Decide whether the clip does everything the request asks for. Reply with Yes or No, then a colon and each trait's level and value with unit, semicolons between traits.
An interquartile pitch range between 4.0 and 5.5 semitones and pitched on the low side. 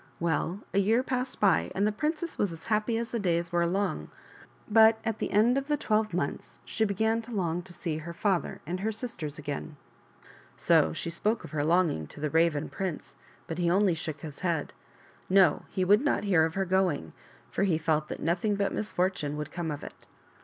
No: average, 4.7 semitones; medium, 185 Hz